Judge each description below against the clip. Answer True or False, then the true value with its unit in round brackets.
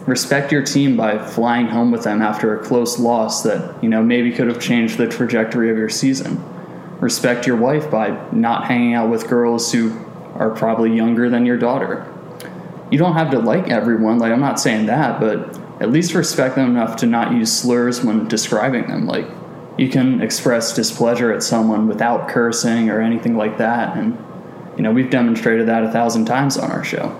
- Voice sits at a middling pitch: False (115 Hz)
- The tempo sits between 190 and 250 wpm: True (195 wpm)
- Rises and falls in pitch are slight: True (1.4 semitones)